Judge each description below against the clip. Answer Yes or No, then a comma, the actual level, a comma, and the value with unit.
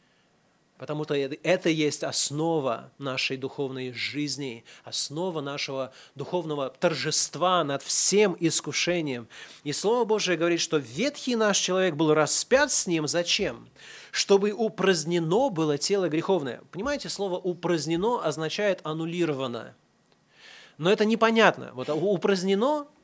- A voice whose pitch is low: No, medium, 165 Hz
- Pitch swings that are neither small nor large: Yes, average, 4.7 semitones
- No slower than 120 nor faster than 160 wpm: No, slow, 110 wpm